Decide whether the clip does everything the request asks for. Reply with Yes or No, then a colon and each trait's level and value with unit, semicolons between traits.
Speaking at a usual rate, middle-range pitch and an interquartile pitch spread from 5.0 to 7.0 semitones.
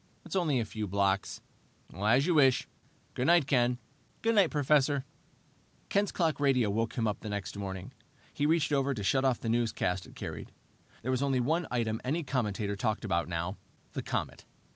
No: average, 180 wpm; low, 125 Hz; wide, 5.6 semitones